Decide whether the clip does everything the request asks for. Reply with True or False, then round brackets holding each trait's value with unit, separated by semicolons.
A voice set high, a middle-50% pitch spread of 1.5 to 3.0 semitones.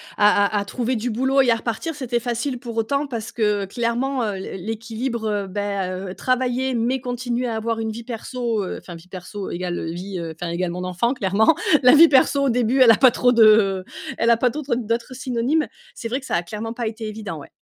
False (230 Hz; 3.5 semitones)